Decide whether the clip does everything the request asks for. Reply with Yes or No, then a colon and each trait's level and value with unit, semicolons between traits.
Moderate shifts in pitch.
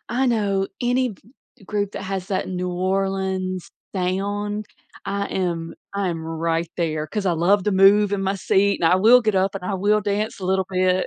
No: narrow, 1.8 semitones